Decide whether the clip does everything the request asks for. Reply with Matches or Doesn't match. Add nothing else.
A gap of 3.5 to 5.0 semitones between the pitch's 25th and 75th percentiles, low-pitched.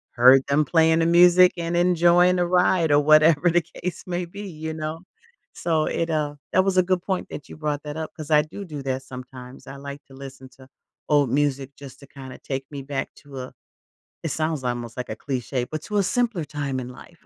Doesn't match